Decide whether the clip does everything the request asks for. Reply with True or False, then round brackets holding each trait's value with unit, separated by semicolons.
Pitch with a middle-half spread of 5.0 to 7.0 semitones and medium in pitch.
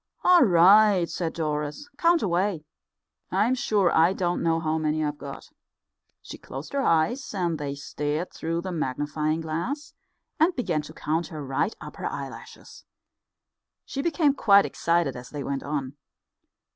True (5.3 semitones; 165 Hz)